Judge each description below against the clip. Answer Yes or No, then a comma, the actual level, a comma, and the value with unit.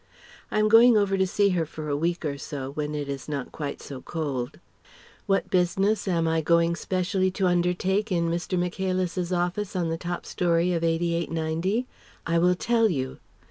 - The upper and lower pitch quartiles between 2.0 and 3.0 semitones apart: Yes, narrow, 2.6 semitones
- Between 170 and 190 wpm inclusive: Yes, average, 185 wpm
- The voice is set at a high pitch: No, medium, 175 Hz